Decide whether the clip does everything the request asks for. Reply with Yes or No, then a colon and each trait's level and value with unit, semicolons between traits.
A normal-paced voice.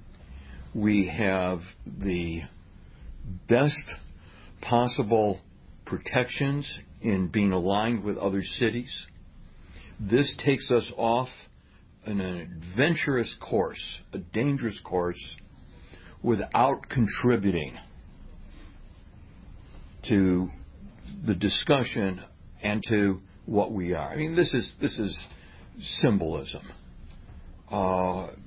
No: slow, 85 wpm